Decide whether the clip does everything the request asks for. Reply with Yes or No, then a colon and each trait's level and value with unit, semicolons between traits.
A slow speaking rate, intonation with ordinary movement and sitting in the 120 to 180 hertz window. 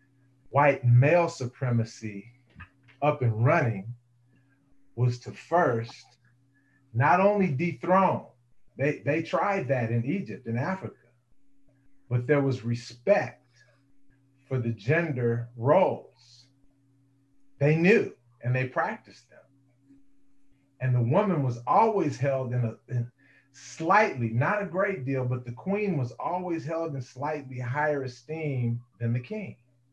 Yes: slow, 120 wpm; average, 3.2 semitones; low, 135 Hz